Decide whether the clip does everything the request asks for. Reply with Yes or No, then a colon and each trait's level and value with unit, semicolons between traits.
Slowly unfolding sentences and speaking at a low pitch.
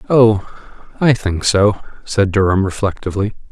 Yes: slow, 120 wpm; low, 100 Hz